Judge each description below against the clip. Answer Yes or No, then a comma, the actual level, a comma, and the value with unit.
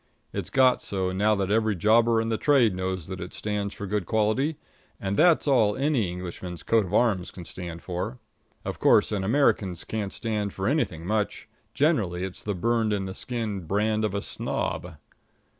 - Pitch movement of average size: Yes, average, 3.4 semitones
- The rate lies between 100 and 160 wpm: No, average, 185 wpm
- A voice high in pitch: No, low, 105 Hz